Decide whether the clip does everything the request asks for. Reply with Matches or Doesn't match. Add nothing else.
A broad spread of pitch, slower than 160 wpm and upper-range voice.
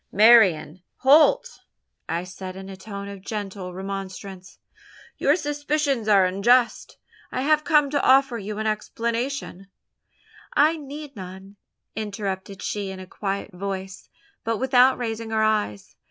Doesn't match